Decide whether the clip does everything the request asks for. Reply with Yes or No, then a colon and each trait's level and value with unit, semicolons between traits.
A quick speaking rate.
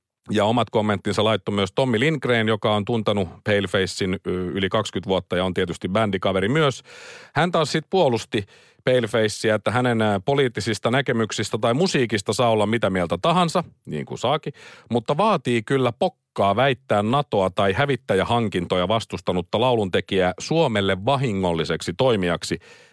No: average, 135 wpm